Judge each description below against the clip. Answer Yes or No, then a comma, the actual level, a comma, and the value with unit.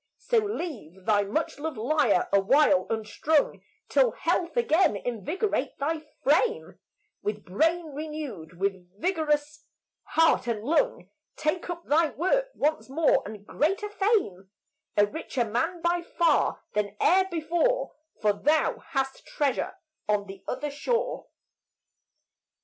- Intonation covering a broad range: Yes, wide, 8.2 semitones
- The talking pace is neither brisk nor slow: No, slow, 125 wpm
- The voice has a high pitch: Yes, very high, 300 Hz